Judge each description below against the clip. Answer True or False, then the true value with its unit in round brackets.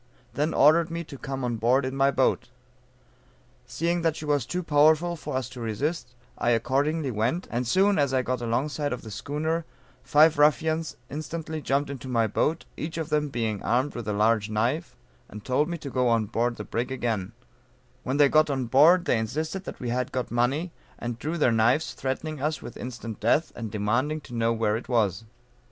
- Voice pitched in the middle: False (130 Hz)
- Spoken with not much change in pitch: False (4.7 semitones)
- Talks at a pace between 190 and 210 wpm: True (205 wpm)